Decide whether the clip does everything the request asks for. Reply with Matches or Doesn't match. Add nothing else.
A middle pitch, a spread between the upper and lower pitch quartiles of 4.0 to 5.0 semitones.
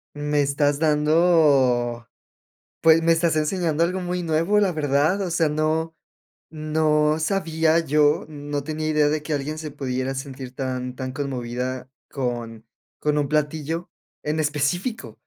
Doesn't match